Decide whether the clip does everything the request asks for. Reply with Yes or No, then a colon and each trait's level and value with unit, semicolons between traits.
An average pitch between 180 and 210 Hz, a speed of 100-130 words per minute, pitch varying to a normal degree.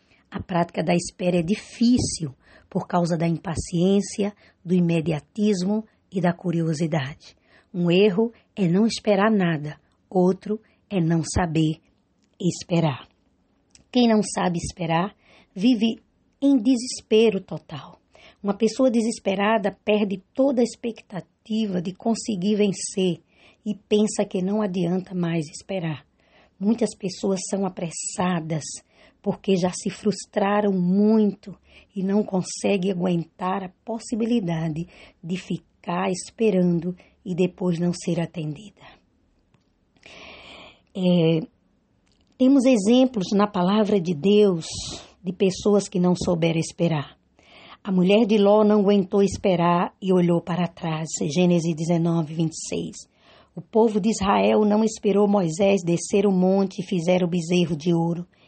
Yes: high, 190 Hz; slow, 120 wpm; average, 3.4 semitones